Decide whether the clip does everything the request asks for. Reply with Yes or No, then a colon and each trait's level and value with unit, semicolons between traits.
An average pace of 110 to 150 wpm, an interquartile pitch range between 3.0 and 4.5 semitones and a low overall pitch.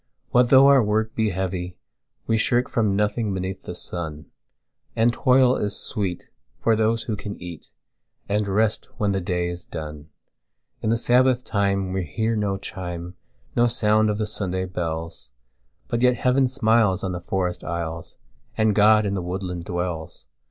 Yes: average, 145 wpm; average, 4.0 semitones; low, 100 Hz